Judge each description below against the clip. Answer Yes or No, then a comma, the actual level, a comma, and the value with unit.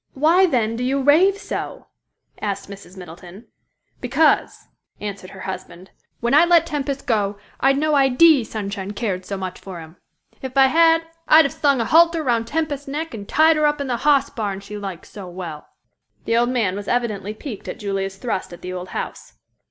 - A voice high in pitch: Yes, high, 235 Hz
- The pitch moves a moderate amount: No, wide, 6.7 semitones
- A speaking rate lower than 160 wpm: No, average, 190 wpm